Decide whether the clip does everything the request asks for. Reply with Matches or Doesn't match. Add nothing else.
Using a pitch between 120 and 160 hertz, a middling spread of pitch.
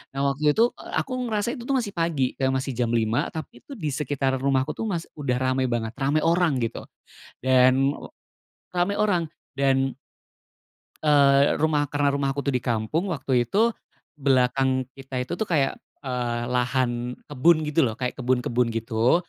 Matches